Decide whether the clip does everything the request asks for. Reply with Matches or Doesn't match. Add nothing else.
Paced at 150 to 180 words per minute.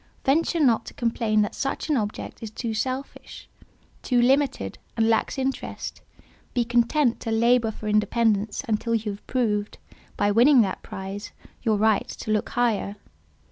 Matches